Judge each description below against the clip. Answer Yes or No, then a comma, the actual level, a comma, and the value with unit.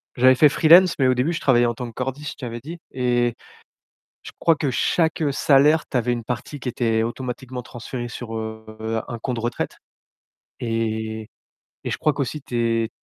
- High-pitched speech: No, low, 125 Hz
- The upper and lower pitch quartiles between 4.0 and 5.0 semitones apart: No, average, 3.2 semitones